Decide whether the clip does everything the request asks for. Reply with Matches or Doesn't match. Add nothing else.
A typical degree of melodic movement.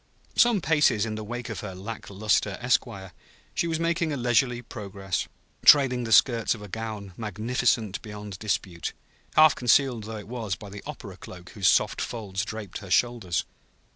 Matches